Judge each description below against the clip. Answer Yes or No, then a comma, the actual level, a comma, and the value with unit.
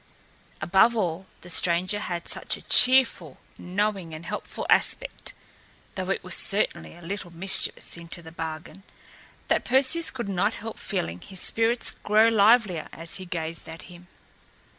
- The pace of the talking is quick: No, average, 150 wpm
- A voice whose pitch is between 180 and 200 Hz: Yes, medium, 185 Hz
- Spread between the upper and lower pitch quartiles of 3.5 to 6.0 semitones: Yes, average, 4.3 semitones